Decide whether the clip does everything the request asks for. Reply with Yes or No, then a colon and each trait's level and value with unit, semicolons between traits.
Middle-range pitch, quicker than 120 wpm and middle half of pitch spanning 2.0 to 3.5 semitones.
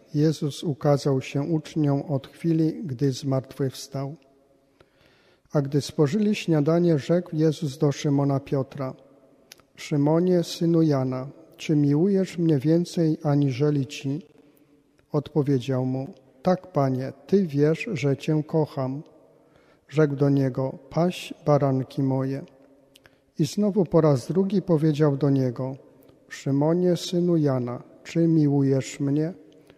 No: medium, 145 Hz; slow, 110 wpm; average, 2.7 semitones